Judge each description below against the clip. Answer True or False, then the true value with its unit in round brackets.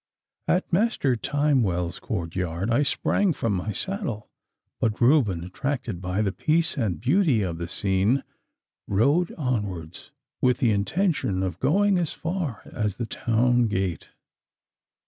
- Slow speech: True (130 wpm)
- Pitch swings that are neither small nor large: False (7.5 semitones)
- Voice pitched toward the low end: True (115 Hz)